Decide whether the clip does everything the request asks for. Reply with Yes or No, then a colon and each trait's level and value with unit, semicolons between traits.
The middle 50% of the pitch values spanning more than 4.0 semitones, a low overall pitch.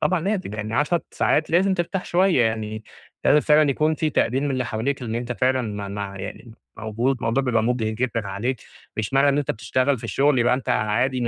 Yes: average, 4.7 semitones; low, 125 Hz